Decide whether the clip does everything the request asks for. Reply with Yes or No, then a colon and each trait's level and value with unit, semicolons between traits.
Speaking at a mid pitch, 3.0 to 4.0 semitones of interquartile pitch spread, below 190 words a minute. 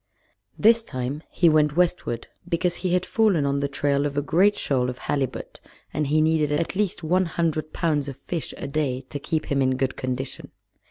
No: medium, 150 Hz; average, 3.7 semitones; average, 200 wpm